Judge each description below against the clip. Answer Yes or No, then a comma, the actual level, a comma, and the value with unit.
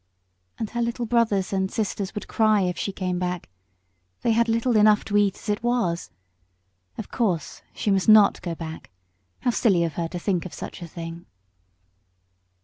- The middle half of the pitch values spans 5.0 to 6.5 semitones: No, average, 4.0 semitones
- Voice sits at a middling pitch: No, high, 200 Hz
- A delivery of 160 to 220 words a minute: Yes, average, 180 wpm